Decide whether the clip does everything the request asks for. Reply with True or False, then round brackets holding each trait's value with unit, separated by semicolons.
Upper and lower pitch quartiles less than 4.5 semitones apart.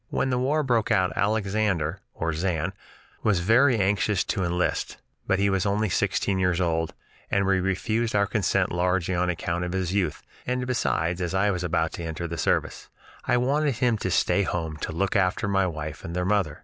True (3.3 semitones)